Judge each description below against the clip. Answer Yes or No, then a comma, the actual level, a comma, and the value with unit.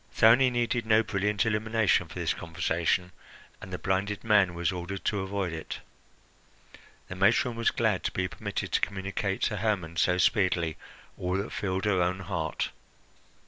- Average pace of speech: Yes, average, 160 wpm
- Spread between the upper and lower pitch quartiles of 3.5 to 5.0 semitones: No, average, 3.0 semitones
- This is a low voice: Yes, very low, 95 Hz